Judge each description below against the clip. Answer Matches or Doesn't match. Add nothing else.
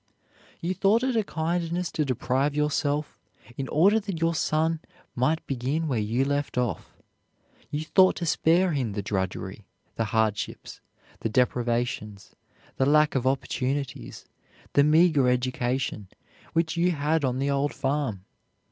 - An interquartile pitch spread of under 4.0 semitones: Doesn't match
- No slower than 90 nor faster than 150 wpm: Matches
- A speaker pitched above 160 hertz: Doesn't match